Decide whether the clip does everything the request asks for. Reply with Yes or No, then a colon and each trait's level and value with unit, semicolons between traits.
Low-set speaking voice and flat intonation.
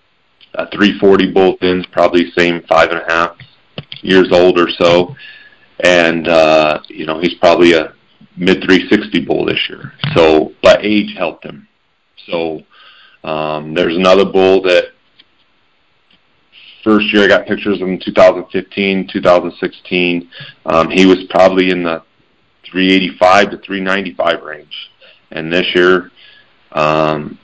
Yes: very low, 90 Hz; narrow, 2.1 semitones